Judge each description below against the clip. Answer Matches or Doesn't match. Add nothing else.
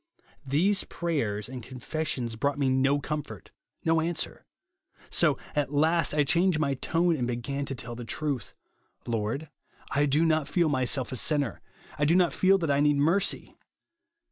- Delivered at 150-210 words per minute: Matches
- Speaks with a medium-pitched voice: Matches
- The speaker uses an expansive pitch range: Doesn't match